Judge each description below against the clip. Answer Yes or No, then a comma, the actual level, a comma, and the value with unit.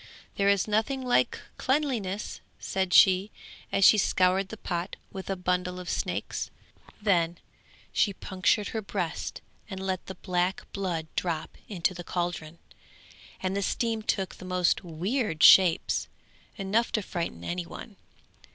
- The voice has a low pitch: No, high, 190 Hz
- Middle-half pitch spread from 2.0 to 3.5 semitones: Yes, narrow, 2.5 semitones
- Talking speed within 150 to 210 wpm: No, average, 140 wpm